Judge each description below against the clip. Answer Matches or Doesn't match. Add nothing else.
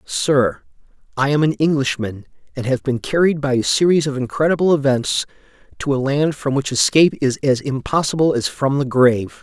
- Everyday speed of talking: Matches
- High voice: Doesn't match